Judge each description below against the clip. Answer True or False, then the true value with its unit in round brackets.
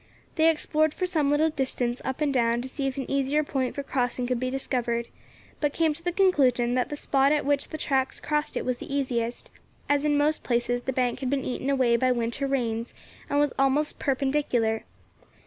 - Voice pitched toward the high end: True (270 Hz)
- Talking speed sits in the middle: False (210 wpm)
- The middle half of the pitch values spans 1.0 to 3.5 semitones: True (3.0 semitones)